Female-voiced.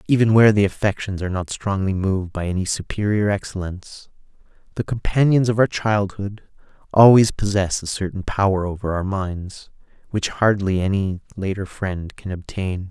No: male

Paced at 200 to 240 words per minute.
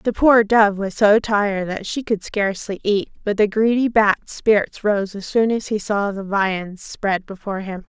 Yes: fast, 205 wpm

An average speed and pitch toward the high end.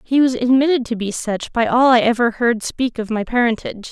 No: fast, 230 wpm; high, 240 Hz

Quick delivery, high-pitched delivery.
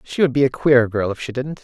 No: fast, 330 wpm; low, 130 Hz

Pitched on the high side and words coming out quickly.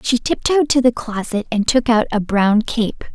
Yes: high, 230 Hz; fast, 210 wpm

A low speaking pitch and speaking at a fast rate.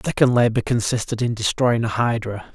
No: low, 115 Hz; average, 190 wpm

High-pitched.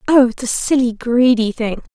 Yes: high, 245 Hz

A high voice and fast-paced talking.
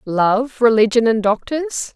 No: high, 235 Hz; slow, 125 wpm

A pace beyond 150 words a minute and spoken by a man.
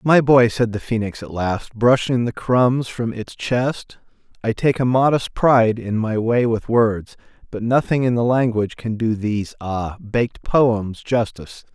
Yes: average, 170 wpm; male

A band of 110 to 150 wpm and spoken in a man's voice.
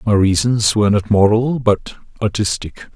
Yes: average, 140 wpm; male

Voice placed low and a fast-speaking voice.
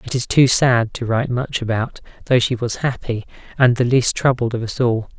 Yes: low, 120 Hz; fast, 220 wpm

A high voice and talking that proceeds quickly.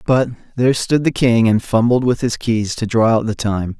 No: low, 115 Hz; fast, 235 wpm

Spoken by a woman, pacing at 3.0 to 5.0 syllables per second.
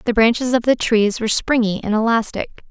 No: female; 5.9 syllables/s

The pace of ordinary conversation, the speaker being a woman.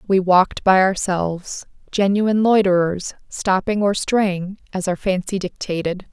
No: slow, 125 wpm; female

